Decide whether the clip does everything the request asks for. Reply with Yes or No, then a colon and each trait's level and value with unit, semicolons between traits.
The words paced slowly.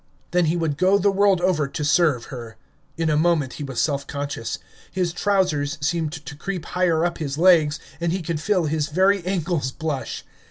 No: average, 195 wpm